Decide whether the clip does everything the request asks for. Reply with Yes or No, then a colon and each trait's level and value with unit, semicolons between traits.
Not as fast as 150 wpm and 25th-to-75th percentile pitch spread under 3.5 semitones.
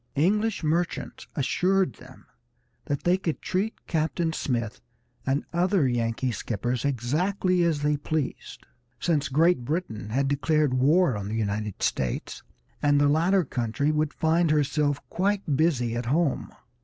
No: average, 140 wpm; average, 5.2 semitones